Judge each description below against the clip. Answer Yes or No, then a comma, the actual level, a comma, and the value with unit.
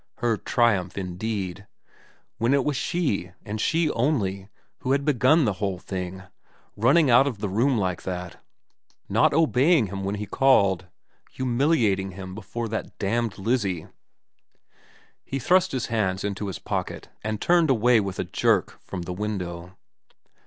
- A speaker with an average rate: Yes, average, 150 wpm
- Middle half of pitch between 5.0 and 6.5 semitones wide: Yes, average, 5.3 semitones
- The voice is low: Yes, low, 105 Hz